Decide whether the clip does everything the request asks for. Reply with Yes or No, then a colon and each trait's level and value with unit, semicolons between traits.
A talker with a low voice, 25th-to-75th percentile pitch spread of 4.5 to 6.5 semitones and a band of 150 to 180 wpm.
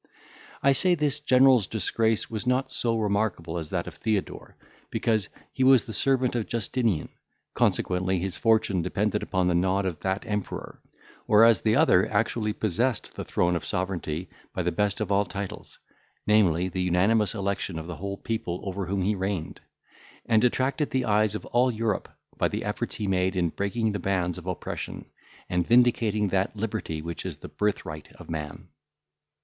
No: low, 100 Hz; average, 3.8 semitones; average, 170 wpm